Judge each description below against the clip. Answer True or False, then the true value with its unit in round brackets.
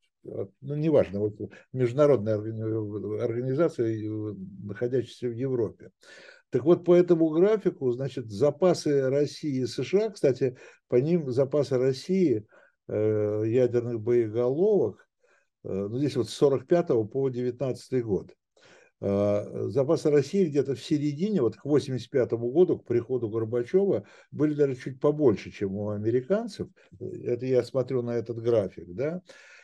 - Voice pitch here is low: True (130 Hz)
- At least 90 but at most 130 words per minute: True (120 wpm)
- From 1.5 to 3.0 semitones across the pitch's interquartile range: False (4.3 semitones)